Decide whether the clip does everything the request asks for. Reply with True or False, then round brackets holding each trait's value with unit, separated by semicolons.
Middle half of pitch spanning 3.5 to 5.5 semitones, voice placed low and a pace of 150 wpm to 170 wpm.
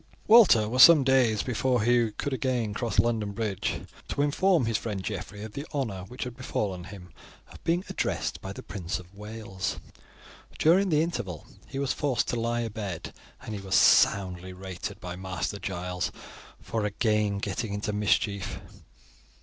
True (4.5 semitones; 105 Hz; 165 wpm)